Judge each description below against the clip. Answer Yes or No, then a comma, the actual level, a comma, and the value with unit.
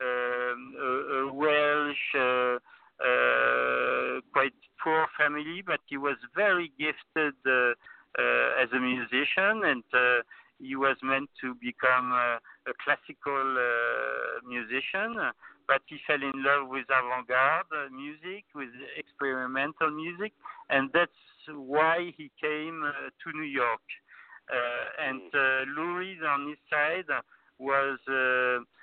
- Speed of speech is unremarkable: No, slow, 125 wpm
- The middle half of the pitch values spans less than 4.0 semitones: Yes, average, 3.2 semitones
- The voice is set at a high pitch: No, low, 135 Hz